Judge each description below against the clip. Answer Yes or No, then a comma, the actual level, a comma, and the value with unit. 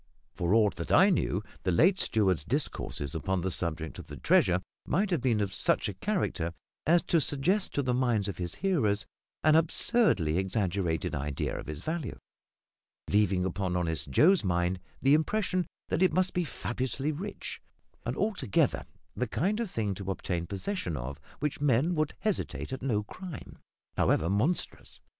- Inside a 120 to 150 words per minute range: No, average, 165 wpm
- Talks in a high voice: No, low, 110 Hz